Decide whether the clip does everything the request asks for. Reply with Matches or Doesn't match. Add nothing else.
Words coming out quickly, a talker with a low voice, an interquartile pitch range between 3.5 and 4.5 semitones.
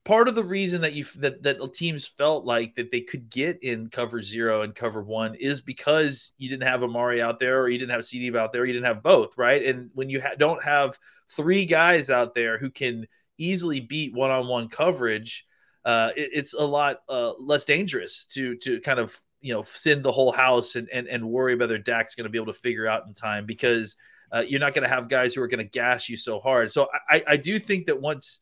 Matches